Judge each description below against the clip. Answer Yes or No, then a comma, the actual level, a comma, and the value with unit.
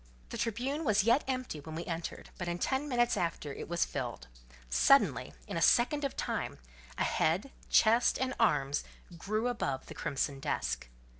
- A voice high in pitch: Yes, high, 215 Hz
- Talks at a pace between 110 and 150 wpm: No, average, 170 wpm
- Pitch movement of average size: No, wide, 8.2 semitones